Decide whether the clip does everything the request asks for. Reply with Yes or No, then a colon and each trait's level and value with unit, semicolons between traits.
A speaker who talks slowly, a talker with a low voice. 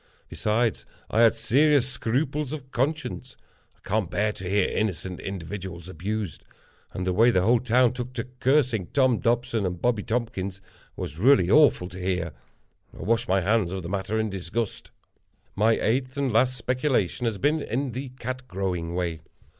No: average, 165 wpm; low, 110 Hz